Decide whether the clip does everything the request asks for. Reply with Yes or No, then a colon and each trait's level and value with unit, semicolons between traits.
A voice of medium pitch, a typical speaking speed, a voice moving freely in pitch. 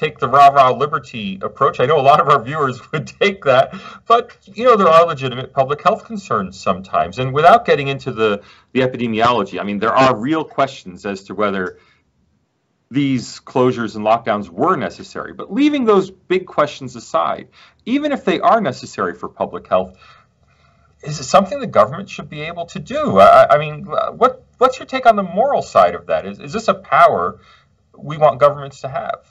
Yes: medium, 150 Hz; average, 190 wpm; wide, 7.5 semitones